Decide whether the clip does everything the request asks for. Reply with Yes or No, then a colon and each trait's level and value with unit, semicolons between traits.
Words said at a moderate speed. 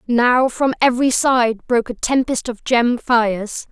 Yes: average, 160 wpm